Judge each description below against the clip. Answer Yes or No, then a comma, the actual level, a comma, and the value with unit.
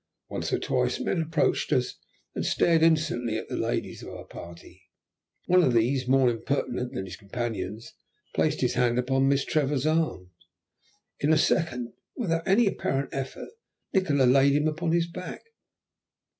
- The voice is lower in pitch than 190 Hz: Yes, low, 135 Hz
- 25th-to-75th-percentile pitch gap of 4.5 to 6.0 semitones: Yes, average, 4.9 semitones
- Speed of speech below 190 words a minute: Yes, average, 160 wpm